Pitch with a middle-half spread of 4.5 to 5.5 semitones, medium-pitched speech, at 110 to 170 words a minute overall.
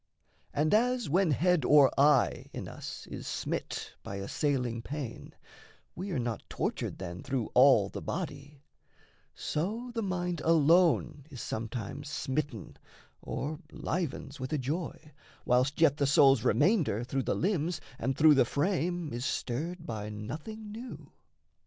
Yes: average, 5.2 semitones; medium, 145 Hz; average, 140 wpm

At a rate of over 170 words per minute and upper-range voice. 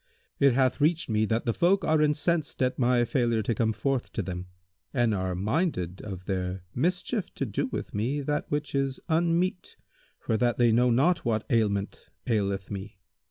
No: average, 180 wpm; low, 120 Hz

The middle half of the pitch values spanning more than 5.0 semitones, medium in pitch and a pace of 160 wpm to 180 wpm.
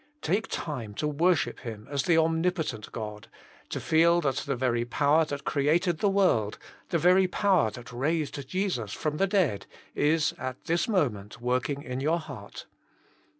Yes: wide, 5.4 semitones; medium, 150 Hz; average, 165 wpm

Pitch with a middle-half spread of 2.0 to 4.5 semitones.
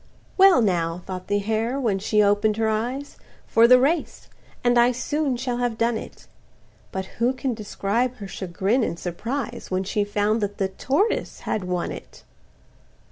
Yes: average, 3.9 semitones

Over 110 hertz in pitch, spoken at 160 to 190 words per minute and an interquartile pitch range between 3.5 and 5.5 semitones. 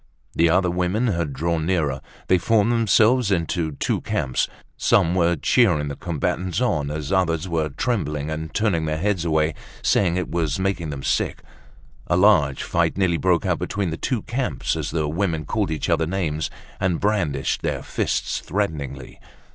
No: very low, 85 Hz; average, 175 wpm; average, 3.8 semitones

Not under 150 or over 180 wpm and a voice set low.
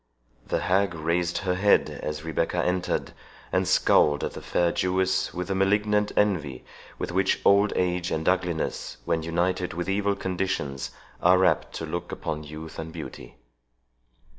Yes: average, 155 wpm; very low, 90 Hz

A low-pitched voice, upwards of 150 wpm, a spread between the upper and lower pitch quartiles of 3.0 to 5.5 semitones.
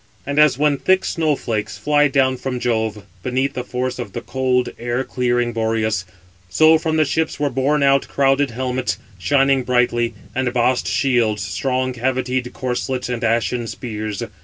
No: low, 125 Hz; average, 160 wpm; narrow, 2.5 semitones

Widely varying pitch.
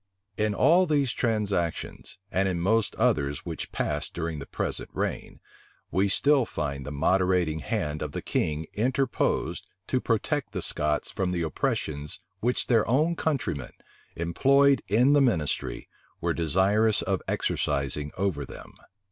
Yes: wide, 7.8 semitones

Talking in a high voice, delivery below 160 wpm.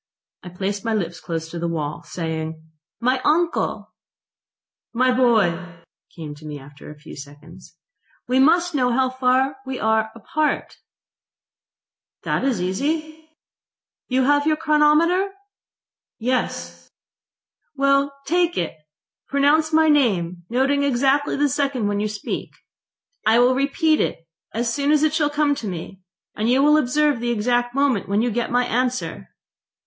Yes: very high, 250 Hz; average, 145 wpm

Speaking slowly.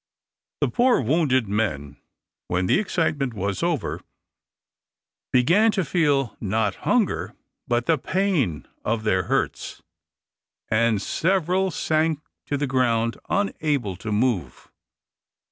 Yes: slow, 110 wpm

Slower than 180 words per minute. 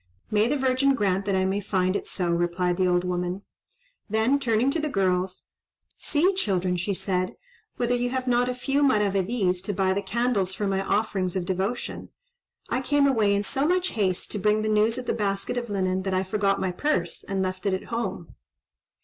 No: average, 200 wpm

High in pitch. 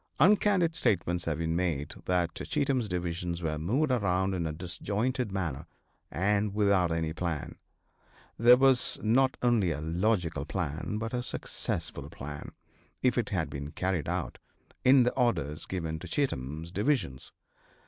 No: very low, 90 Hz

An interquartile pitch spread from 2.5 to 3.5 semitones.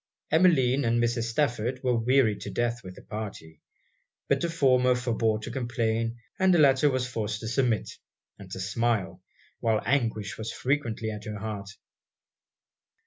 Yes: average, 2.9 semitones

